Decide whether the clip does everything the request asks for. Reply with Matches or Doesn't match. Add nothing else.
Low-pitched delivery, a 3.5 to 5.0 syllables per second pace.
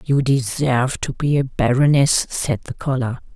Matches